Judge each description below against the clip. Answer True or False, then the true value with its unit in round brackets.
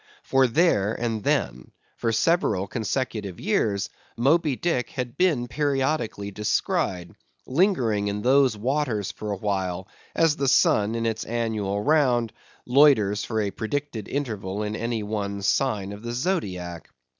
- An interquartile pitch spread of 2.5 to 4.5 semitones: False (4.9 semitones)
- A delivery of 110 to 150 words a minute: True (135 wpm)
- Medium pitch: False (115 Hz)